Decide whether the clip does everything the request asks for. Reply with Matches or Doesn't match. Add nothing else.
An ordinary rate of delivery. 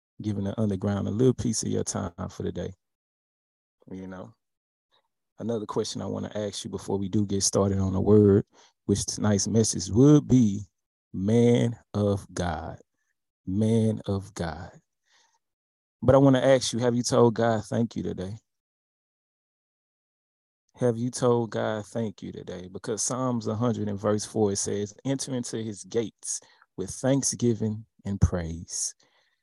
Matches